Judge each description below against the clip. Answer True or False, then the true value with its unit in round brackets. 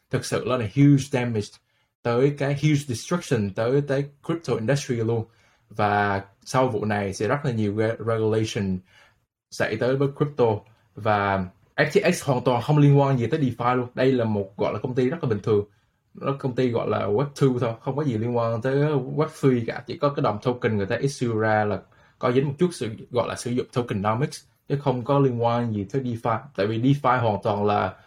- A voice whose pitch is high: False (120 Hz)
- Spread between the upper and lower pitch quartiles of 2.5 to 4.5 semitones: True (4.2 semitones)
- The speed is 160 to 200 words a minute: False (210 wpm)